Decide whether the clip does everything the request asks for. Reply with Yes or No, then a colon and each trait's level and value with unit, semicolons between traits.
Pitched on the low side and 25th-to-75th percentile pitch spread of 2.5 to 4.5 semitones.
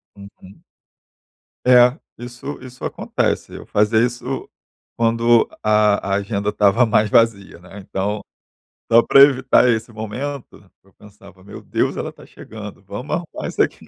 Yes: low, 110 Hz; average, 3.2 semitones